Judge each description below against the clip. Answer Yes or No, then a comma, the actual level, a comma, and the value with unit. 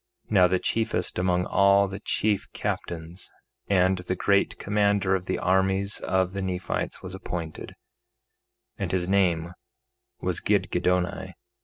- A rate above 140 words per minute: No, slow, 135 wpm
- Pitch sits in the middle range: No, very low, 95 Hz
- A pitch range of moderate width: No, narrow, 1.6 semitones